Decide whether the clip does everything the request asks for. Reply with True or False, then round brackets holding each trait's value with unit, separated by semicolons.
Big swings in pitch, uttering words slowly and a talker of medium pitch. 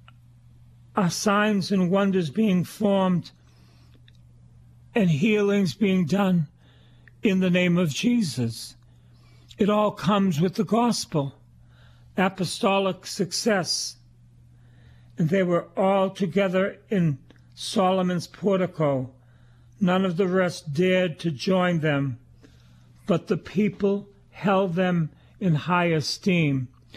True (8.9 semitones; 105 wpm; 170 Hz)